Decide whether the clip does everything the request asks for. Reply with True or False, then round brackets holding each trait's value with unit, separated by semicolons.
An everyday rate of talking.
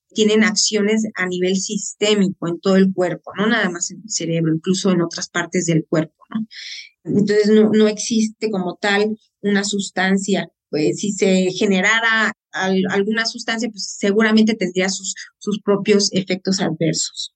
True (150 wpm)